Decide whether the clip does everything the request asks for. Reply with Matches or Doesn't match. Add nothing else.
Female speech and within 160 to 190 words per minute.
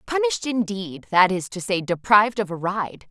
Matches